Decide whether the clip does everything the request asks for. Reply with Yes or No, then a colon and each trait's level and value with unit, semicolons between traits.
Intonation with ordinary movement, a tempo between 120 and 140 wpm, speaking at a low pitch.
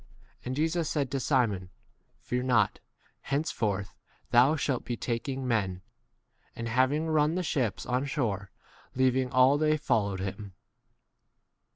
Yes: average, 4.6 semitones; slow, 135 wpm; low, 130 Hz